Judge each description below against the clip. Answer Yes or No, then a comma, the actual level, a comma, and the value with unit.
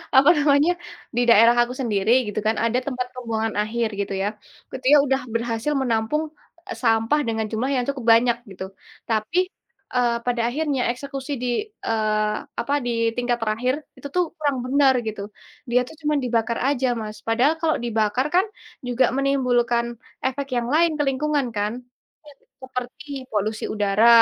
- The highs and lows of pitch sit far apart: No, average, 3.6 semitones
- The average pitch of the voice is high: Yes, high, 245 Hz